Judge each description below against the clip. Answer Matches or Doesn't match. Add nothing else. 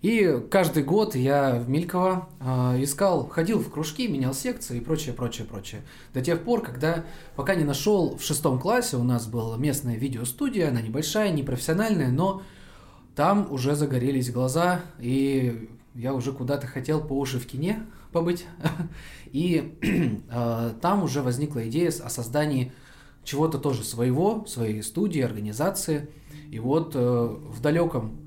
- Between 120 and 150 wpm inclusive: Matches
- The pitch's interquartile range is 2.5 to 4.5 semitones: Doesn't match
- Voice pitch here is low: Doesn't match